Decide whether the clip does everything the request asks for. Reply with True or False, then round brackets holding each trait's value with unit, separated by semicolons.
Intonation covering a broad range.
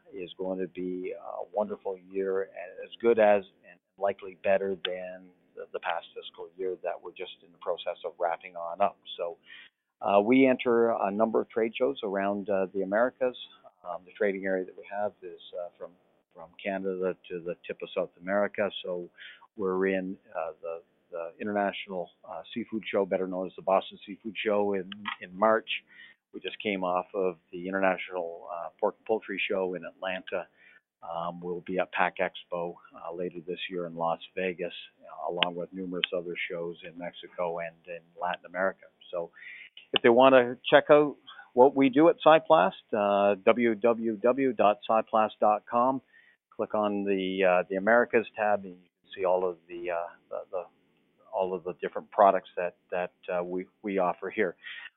False (4.3 semitones)